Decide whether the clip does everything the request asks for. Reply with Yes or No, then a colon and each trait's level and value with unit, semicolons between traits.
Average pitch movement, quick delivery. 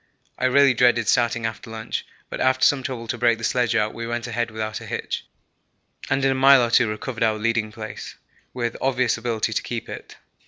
No: narrow, 2.1 semitones; fast, 210 wpm